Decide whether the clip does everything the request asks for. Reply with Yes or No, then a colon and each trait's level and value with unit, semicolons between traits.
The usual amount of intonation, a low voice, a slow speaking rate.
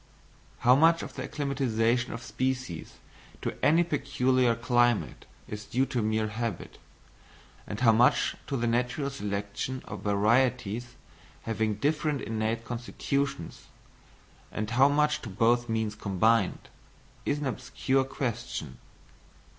Yes: average, 3.4 semitones; low, 120 Hz; slow, 125 wpm